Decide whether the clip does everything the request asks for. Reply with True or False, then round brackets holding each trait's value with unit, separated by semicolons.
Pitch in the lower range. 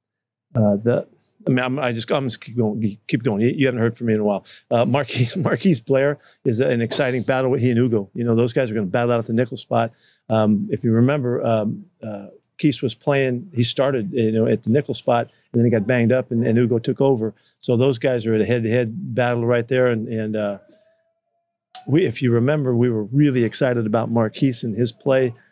True (120 Hz)